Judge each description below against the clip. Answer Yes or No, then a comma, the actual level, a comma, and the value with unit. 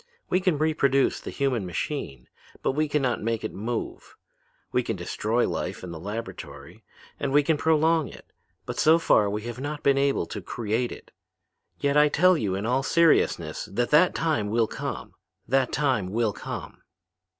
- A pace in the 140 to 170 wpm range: No, average, 180 wpm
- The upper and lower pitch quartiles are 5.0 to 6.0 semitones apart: Yes, wide, 5.4 semitones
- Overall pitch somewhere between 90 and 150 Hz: Yes, low, 135 Hz